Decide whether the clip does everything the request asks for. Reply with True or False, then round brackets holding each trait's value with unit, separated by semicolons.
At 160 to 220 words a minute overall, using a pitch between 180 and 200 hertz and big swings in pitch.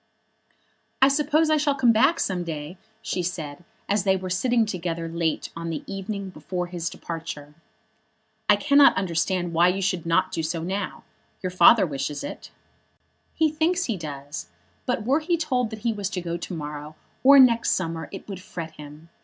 True (180 wpm; 185 Hz; 5.9 semitones)